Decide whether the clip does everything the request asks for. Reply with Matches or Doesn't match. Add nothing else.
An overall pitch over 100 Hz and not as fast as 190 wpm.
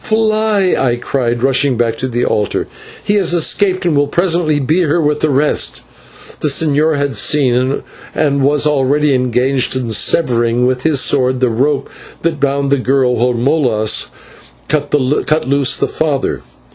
Matches